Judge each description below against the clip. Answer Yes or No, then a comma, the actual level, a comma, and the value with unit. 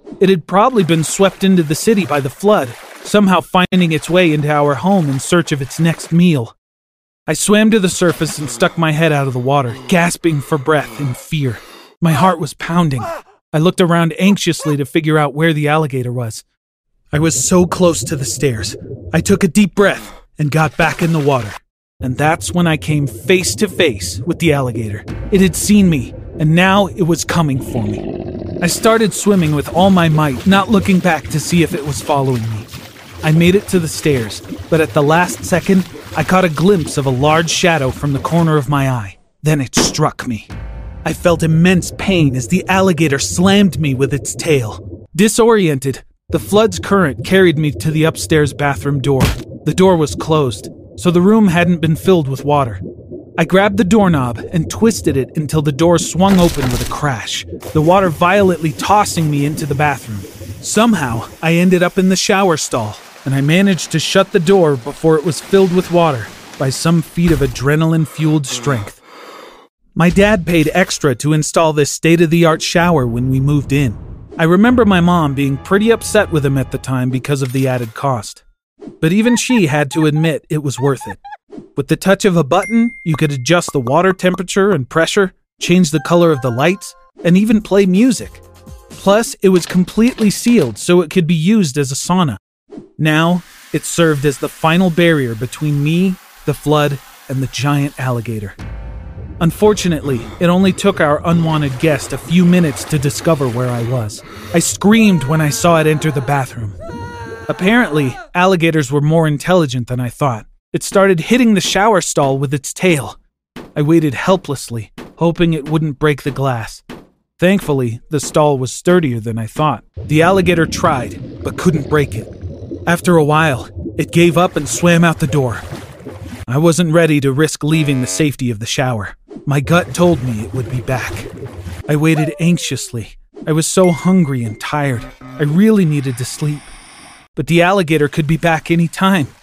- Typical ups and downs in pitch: Yes, average, 4.7 semitones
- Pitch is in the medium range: Yes, medium, 155 Hz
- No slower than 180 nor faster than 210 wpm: Yes, average, 190 wpm